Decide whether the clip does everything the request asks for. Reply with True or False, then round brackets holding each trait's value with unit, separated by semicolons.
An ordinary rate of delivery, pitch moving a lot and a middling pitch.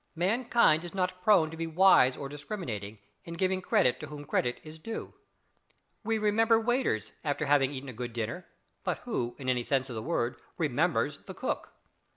True (185 wpm; 6.9 semitones; 155 Hz)